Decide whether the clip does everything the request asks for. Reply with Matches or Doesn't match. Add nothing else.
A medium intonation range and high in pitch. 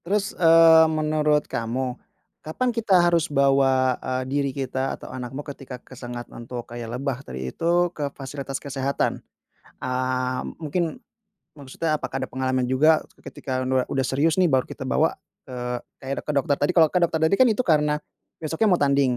Doesn't match